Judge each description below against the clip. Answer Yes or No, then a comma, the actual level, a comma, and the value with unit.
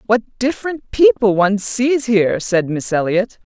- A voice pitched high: Yes, high, 210 Hz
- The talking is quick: No, average, 150 wpm